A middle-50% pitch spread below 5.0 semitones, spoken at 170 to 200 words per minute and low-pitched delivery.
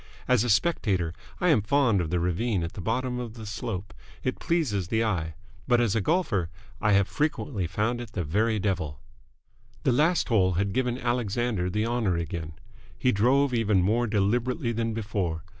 Yes: average, 4.5 semitones; average, 180 wpm; low, 110 Hz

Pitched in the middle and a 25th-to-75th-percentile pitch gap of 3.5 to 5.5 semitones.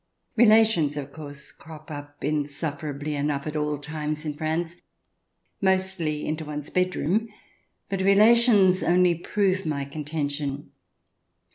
Yes: medium, 155 Hz; average, 4.1 semitones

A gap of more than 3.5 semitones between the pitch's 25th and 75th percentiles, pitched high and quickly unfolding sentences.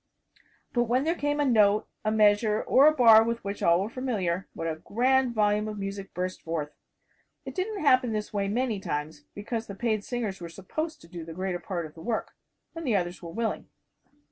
Yes: average, 4.8 semitones; high, 210 Hz; fast, 210 wpm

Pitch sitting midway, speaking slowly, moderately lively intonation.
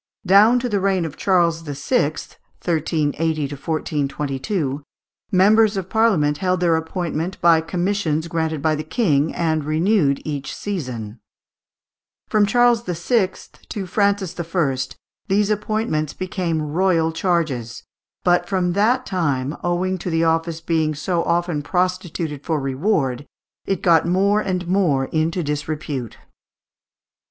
Yes: medium, 170 Hz; slow, 125 wpm; average, 3.7 semitones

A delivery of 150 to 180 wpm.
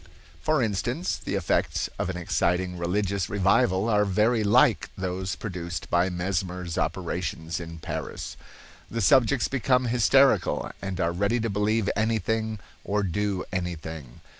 No: slow, 135 wpm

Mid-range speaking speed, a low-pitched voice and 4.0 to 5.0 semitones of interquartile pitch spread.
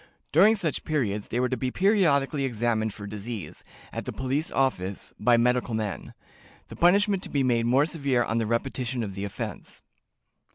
Yes: average, 175 wpm; low, 125 Hz; average, 4.5 semitones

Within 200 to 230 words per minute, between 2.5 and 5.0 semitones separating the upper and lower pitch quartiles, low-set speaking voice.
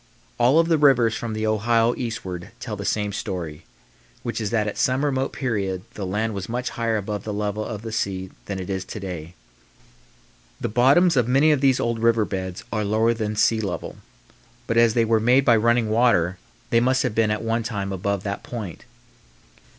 Yes: fast, 205 wpm; average, 2.8 semitones; low, 110 Hz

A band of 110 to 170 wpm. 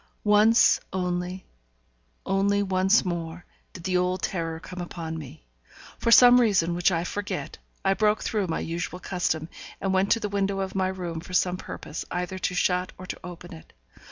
No: average, 180 wpm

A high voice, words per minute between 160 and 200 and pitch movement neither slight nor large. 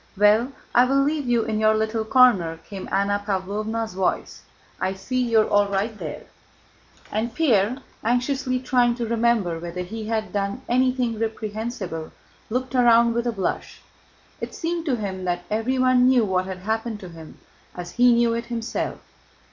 Yes: high, 225 Hz; average, 165 wpm; average, 3.6 semitones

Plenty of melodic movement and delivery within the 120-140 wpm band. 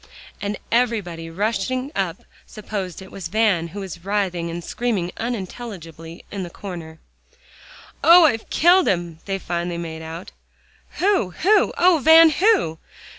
Yes: wide, 6.1 semitones; slow, 135 wpm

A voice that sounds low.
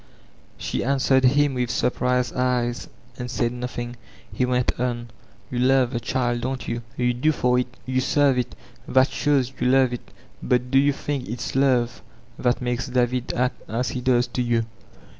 Yes: low, 125 Hz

